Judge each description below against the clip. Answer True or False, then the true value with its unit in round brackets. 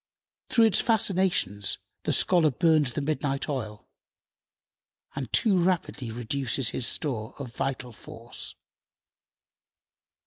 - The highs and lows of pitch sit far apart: True (6.1 semitones)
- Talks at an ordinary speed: False (105 wpm)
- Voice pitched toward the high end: False (135 Hz)